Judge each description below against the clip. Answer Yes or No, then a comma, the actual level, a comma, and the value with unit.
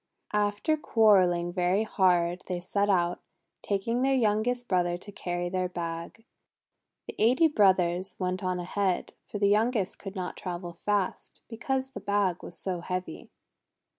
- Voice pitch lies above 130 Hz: Yes, high, 190 Hz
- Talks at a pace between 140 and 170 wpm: Yes, average, 145 wpm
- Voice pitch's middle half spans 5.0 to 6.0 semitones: No, average, 3.0 semitones